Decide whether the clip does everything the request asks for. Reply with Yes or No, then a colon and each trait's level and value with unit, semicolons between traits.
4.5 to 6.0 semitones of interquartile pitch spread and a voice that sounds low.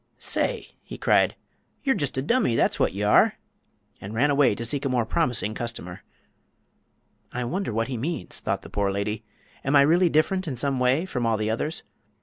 Yes: average, 5.1 semitones; low, 125 Hz